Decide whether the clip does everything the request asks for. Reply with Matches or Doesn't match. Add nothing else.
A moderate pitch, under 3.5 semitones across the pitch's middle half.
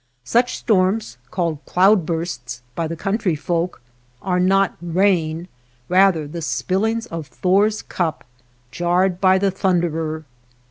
Matches